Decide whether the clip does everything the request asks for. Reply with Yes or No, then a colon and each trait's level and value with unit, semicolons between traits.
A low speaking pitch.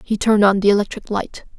No: high, 205 Hz